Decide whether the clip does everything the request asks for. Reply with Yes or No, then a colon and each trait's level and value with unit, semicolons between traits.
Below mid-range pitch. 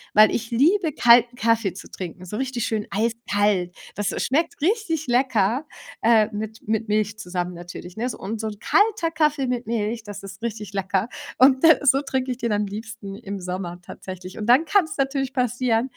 No: high, 225 Hz